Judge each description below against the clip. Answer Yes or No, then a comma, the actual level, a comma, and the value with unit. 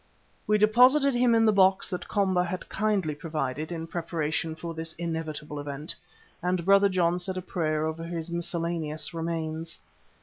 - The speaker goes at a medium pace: Yes, average, 160 wpm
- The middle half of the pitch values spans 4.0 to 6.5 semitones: No, average, 3.0 semitones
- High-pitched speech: No, medium, 170 Hz